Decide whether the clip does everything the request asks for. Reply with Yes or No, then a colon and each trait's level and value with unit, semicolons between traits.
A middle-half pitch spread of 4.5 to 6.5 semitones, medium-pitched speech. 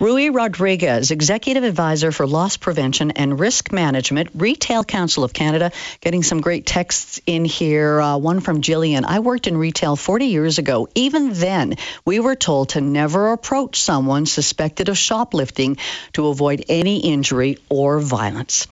Yes: average, 5.3 semitones; medium, 165 Hz